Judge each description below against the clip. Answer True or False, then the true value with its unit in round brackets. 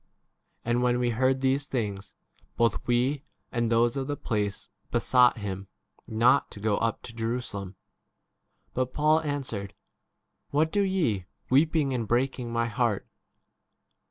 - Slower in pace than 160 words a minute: True (140 wpm)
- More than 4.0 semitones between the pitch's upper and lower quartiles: False (3.3 semitones)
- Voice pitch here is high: False (120 Hz)